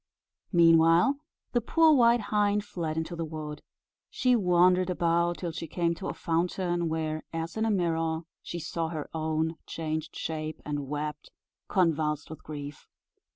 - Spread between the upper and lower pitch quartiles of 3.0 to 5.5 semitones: No, narrow, 2.4 semitones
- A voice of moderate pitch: Yes, medium, 165 Hz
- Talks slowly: No, average, 155 wpm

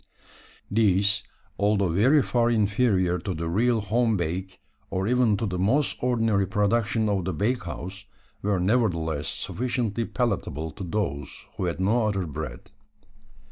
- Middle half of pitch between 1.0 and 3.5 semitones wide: No, average, 4.0 semitones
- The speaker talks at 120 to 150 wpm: Yes, average, 140 wpm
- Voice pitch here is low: Yes, low, 100 Hz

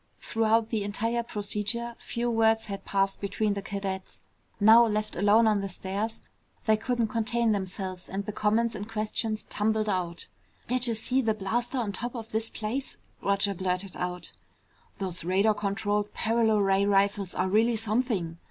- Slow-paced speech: No, average, 160 wpm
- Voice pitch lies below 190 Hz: No, high, 210 Hz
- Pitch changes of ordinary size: No, narrow, 2.3 semitones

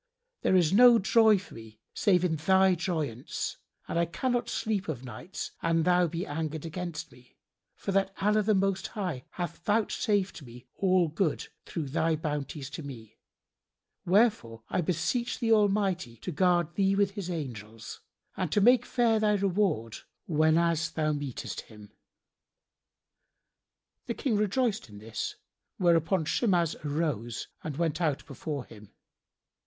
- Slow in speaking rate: No, average, 150 wpm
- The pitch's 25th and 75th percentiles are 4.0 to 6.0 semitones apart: Yes, average, 5.1 semitones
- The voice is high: No, medium, 170 Hz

